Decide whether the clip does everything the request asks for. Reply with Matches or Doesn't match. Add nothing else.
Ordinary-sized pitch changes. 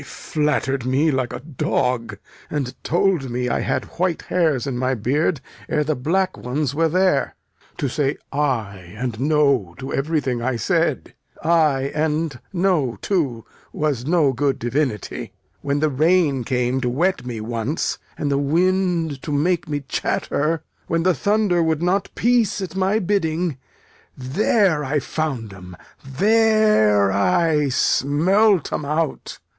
Matches